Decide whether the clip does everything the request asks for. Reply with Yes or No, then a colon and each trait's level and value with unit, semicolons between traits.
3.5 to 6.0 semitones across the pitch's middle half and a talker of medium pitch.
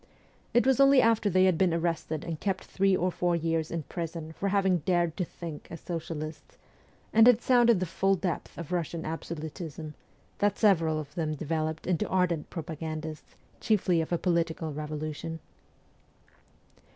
No: average, 3.0 semitones; medium, 170 Hz